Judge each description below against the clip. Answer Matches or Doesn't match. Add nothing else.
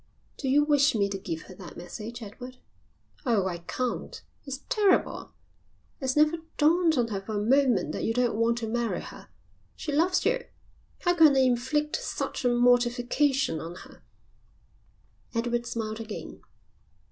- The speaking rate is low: Doesn't match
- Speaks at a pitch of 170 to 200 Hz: Doesn't match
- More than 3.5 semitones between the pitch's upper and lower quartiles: Matches